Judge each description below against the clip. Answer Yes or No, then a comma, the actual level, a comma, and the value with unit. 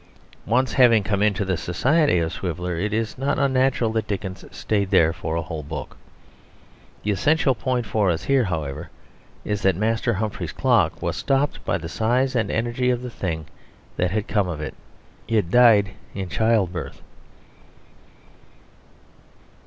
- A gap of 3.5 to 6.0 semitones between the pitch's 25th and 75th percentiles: Yes, average, 5.3 semitones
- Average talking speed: Yes, average, 155 wpm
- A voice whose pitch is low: Yes, low, 105 Hz